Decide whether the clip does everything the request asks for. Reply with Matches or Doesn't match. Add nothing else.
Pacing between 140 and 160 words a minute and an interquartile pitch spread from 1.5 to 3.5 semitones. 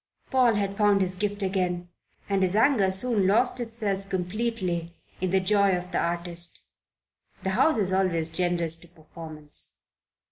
Matches